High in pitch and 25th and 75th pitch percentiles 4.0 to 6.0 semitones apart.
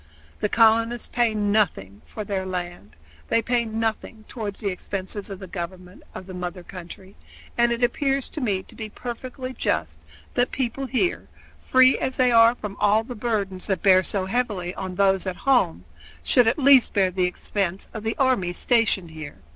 Yes: high, 210 Hz; average, 4.3 semitones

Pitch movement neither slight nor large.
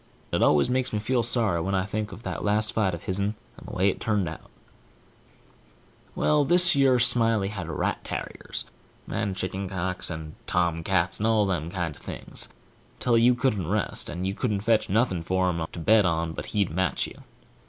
Yes: average, 4.2 semitones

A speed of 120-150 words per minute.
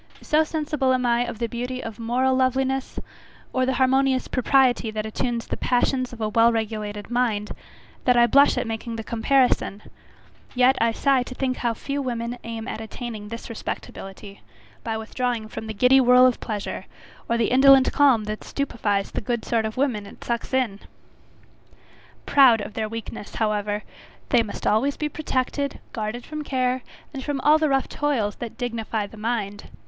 No: average, 175 wpm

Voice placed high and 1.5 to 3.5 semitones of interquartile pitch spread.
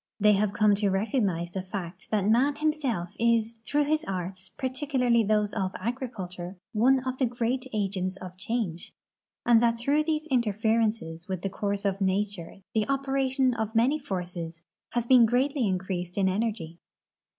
No: high, 215 Hz; average, 4.9 semitones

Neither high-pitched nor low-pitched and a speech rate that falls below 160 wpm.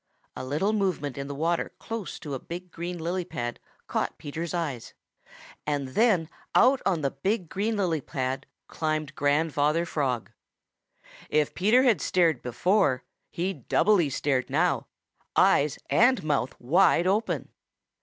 Yes: medium, 160 Hz; average, 140 wpm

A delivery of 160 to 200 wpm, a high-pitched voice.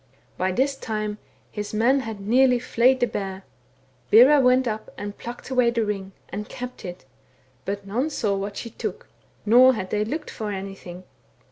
Yes: average, 170 wpm; high, 220 Hz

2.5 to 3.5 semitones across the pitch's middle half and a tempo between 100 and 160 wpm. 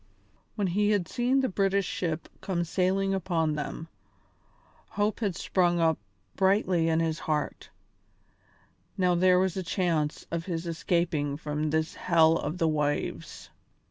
Yes: average, 3.0 semitones; average, 145 wpm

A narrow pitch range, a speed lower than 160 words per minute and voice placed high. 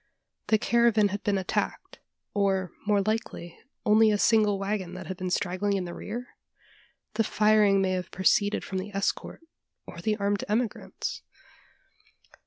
Yes: narrow, 2.2 semitones; average, 150 wpm; high, 205 Hz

